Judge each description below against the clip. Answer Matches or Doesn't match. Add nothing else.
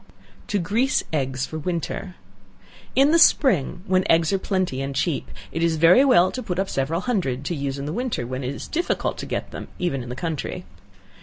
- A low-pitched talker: Doesn't match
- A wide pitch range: Matches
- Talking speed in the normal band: Doesn't match